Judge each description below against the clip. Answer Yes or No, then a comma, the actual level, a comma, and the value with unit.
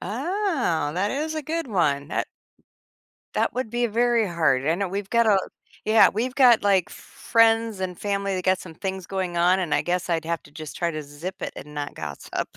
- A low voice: No, high, 190 Hz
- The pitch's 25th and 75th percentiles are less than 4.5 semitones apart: No, average, 5.3 semitones